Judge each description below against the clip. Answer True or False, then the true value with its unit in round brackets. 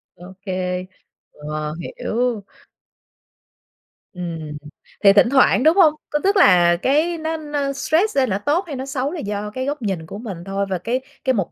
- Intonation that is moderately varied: False (8.0 semitones)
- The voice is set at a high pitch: True (230 Hz)